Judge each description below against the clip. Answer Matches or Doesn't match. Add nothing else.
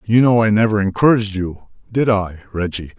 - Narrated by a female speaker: Doesn't match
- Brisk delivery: Doesn't match